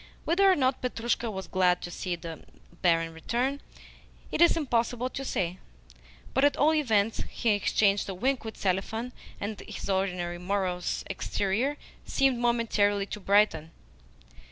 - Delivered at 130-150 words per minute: Yes, average, 145 wpm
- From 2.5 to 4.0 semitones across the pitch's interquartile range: No, average, 5.2 semitones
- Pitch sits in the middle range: No, high, 205 Hz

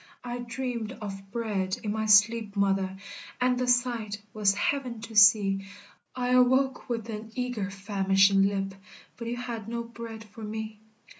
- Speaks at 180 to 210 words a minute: No, average, 155 wpm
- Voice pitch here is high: Yes, high, 220 Hz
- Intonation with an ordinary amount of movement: Yes, average, 3.3 semitones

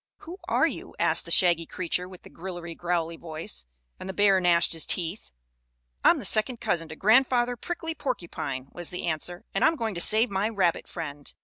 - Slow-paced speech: No, average, 195 wpm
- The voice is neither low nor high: Yes, medium, 180 Hz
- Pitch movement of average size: Yes, average, 4.7 semitones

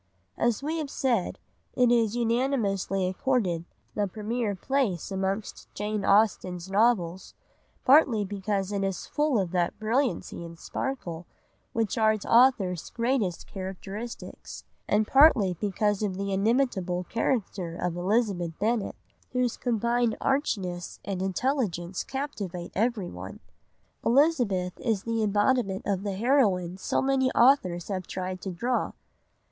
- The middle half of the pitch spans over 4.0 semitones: Yes, average, 4.5 semitones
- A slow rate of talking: Yes, slow, 125 wpm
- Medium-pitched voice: No, high, 205 Hz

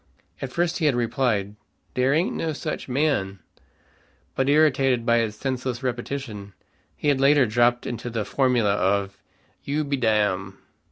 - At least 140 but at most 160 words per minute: Yes, average, 150 wpm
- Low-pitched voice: Yes, low, 125 Hz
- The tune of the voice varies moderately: Yes, average, 4.6 semitones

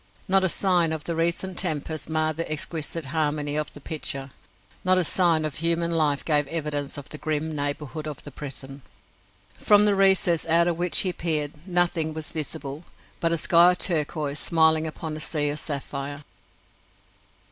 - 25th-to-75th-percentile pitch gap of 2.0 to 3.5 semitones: Yes, narrow, 2.4 semitones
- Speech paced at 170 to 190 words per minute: Yes, average, 175 wpm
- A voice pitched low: No, medium, 155 Hz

